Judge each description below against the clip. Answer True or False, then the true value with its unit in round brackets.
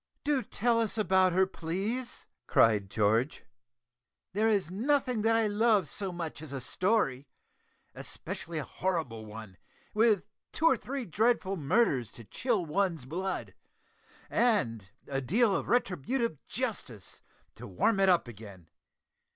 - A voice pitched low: False (190 Hz)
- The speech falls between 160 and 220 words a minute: False (135 wpm)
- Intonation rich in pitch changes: True (8.8 semitones)